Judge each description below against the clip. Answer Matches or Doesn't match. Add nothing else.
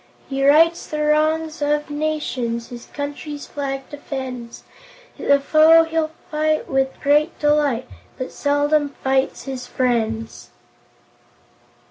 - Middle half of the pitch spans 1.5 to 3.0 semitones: Matches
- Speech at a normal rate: Doesn't match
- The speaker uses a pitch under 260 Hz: Doesn't match